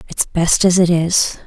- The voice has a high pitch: No, medium, 175 Hz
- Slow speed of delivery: No, fast, 205 wpm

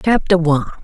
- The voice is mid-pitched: Yes, medium, 175 Hz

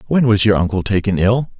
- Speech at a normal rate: No, fast, 225 wpm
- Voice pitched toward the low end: Yes, low, 105 Hz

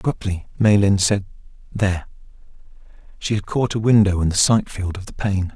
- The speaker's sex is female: No, male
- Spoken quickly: No, average, 175 wpm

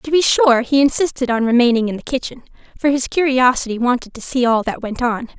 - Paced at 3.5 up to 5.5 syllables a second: No, 5.9 syllables/s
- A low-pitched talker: No, very high, 255 Hz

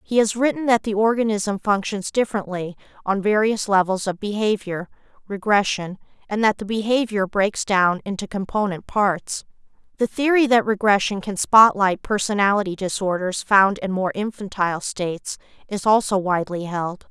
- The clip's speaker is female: Yes, female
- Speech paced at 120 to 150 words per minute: Yes, average, 140 wpm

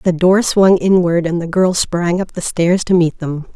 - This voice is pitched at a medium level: Yes, medium, 175 Hz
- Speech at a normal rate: No, fast, 235 wpm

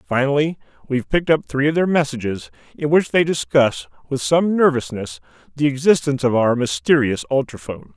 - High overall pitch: No, low, 130 Hz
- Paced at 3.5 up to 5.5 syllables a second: No, 5.8 syllables/s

